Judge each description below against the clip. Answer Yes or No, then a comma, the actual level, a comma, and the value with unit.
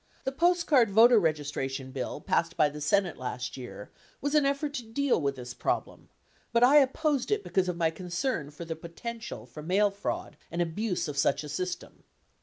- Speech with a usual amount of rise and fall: No, wide, 8.8 semitones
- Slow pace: No, average, 195 wpm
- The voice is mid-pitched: Yes, medium, 180 Hz